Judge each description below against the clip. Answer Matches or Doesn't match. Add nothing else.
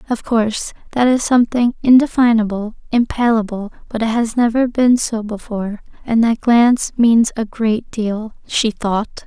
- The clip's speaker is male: Doesn't match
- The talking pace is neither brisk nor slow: Matches